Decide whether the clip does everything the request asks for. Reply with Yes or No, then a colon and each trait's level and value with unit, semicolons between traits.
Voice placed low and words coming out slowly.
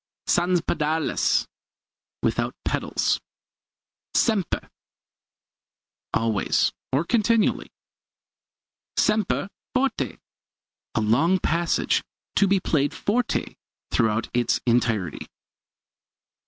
No: medium, 165 Hz; slow, 75 wpm